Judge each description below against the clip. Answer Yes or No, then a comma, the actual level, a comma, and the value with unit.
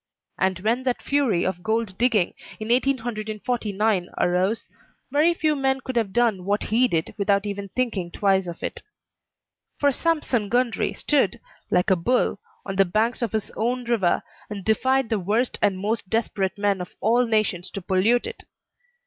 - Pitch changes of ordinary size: Yes, average, 4.1 semitones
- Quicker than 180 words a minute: No, average, 165 wpm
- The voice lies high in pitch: Yes, high, 215 Hz